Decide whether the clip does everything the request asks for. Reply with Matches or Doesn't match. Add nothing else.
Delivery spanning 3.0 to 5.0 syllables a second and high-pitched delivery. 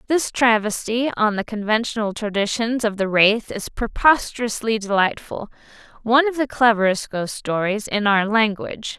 Matches